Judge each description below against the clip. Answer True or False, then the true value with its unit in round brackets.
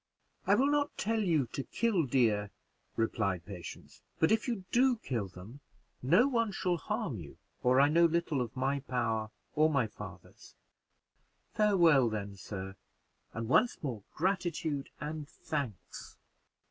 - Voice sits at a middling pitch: True (145 Hz)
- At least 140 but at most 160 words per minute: True (145 wpm)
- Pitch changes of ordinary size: False (8.9 semitones)